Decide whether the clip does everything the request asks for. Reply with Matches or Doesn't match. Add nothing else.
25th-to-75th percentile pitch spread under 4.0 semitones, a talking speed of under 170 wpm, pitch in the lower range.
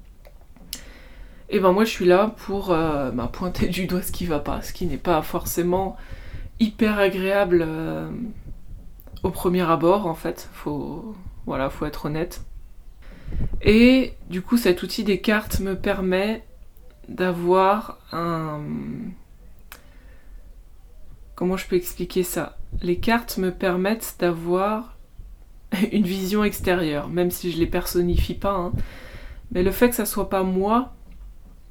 Doesn't match